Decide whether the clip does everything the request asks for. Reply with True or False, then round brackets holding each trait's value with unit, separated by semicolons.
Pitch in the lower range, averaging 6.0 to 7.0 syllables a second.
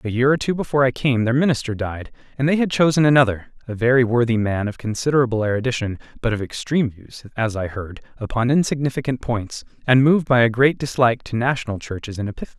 True (125 Hz; 6.6 syllables/s)